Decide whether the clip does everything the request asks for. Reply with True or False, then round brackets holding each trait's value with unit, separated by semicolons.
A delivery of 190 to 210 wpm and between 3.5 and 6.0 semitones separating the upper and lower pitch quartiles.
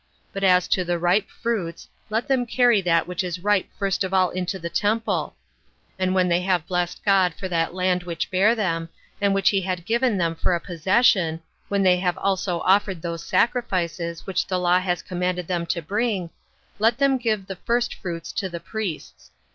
False (195 wpm; 2.7 semitones)